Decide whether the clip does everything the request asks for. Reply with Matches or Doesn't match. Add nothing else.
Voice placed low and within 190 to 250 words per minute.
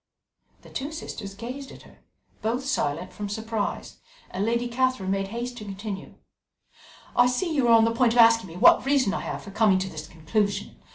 Doesn't match